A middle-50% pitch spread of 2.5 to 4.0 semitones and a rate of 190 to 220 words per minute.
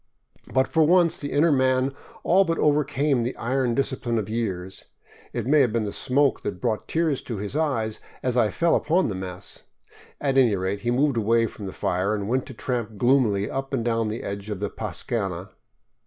No: average, 4.7 semitones; average, 200 wpm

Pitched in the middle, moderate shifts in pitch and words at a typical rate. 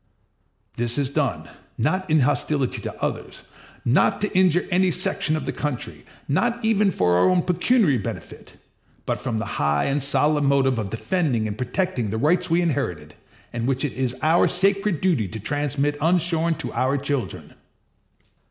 No: medium, 145 Hz; wide, 6.3 semitones; average, 165 wpm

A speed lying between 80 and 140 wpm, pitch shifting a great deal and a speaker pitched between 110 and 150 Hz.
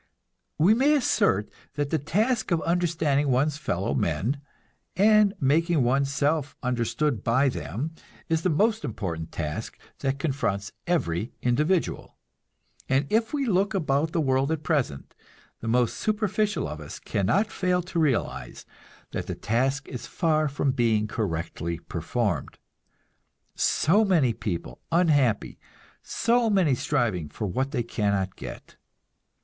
Yes: slow, 135 wpm; wide, 7.1 semitones; medium, 140 Hz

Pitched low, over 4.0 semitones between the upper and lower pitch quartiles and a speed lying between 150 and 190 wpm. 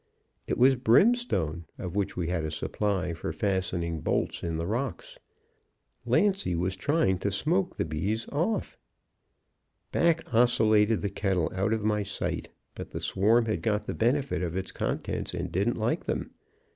Yes: low, 105 Hz; average, 5.1 semitones; average, 160 wpm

